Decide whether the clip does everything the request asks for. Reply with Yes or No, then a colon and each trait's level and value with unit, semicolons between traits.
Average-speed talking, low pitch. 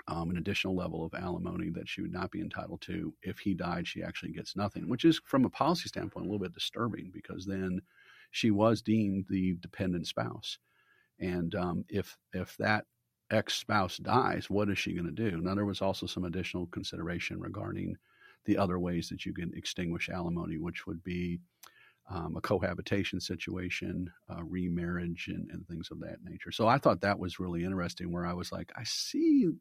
Yes: average, 195 wpm; very low, 90 Hz